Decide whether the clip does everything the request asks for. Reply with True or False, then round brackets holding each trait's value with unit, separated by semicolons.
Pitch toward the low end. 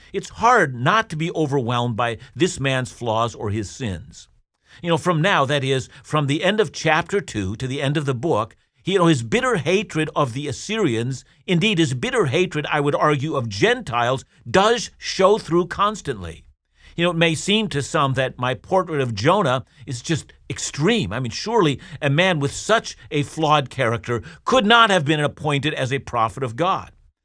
False (145 Hz)